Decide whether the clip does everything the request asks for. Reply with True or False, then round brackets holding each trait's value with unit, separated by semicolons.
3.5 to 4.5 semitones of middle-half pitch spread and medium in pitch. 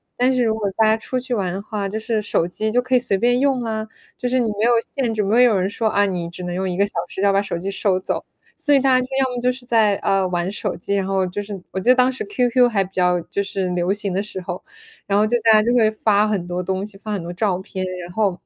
False (3.8 semitones; 205 Hz)